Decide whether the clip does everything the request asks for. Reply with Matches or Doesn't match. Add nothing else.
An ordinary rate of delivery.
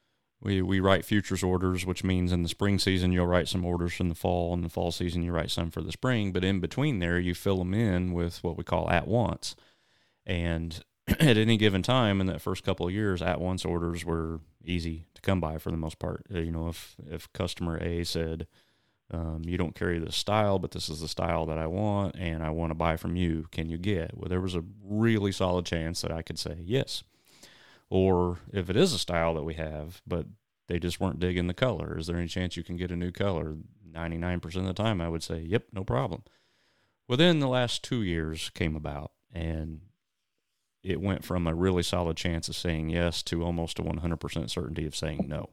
Doesn't match